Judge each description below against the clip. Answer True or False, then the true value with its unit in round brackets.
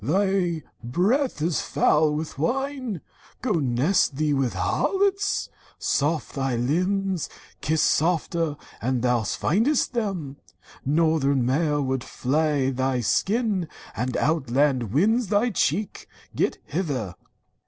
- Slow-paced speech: True (120 wpm)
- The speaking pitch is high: False (155 Hz)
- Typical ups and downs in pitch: False (6.5 semitones)